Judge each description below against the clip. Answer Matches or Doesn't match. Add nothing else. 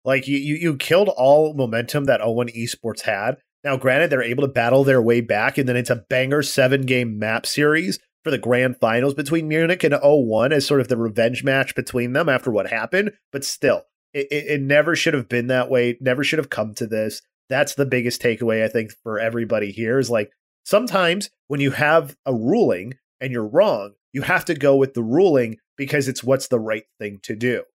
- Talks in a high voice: Doesn't match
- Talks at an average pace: Doesn't match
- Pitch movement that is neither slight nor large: Matches